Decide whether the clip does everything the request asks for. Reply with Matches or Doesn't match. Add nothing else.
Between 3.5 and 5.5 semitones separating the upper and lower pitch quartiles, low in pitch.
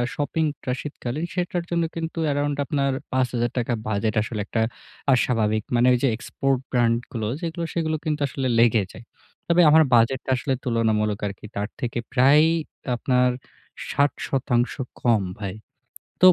Matches